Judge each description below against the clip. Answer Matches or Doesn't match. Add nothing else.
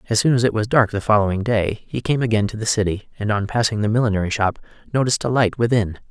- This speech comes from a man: Matches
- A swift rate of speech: Matches